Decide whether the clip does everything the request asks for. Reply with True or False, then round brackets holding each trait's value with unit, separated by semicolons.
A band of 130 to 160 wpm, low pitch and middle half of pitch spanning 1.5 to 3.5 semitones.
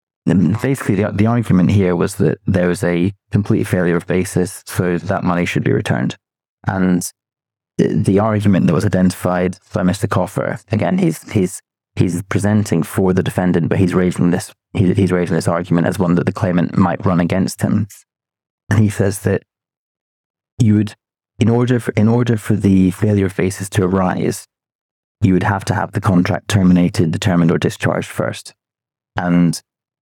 False (170 wpm; 95 Hz; 2.9 semitones)